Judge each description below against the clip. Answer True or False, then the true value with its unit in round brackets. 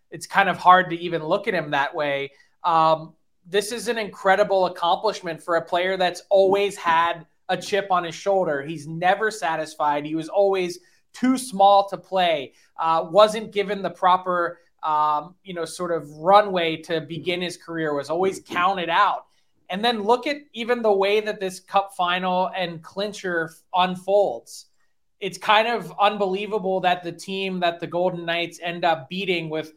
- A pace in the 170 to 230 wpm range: True (175 wpm)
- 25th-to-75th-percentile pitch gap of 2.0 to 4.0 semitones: True (3.1 semitones)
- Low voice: False (180 Hz)